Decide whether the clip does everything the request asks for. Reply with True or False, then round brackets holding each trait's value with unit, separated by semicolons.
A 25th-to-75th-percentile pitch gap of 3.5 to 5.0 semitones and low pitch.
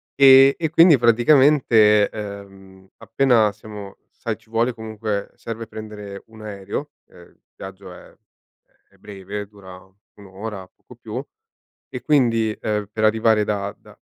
False (2.4 semitones; 110 Hz)